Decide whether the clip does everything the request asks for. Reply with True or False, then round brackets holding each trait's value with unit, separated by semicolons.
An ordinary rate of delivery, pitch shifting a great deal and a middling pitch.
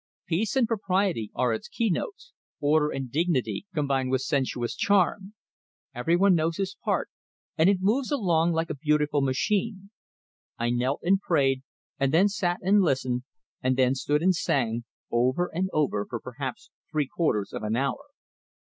True (160 wpm; 6.5 semitones; 155 Hz)